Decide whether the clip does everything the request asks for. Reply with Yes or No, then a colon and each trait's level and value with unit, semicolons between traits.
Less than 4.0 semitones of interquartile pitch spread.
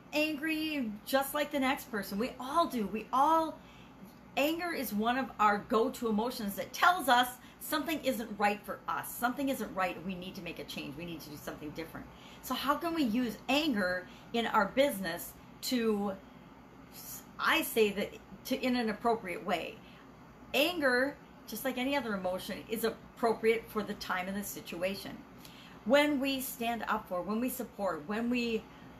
No: average, 4.8 semitones